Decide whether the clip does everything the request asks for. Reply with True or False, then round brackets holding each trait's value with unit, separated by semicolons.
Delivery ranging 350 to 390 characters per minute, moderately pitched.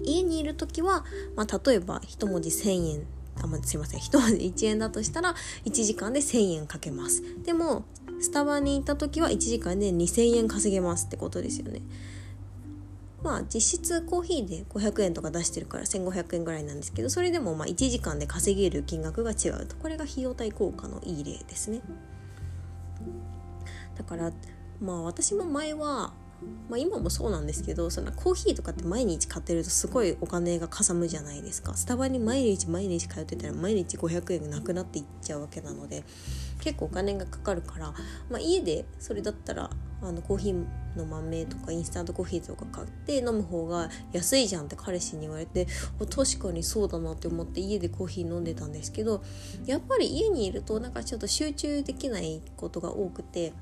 True (375 characters per minute; 175 Hz)